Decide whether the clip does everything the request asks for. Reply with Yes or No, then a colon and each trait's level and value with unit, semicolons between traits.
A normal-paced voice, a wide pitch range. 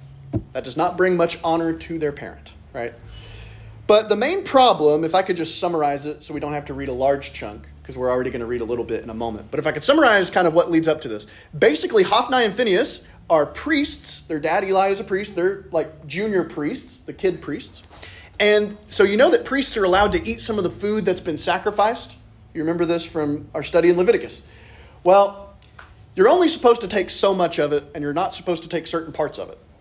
No: fast, 235 wpm; wide, 6.3 semitones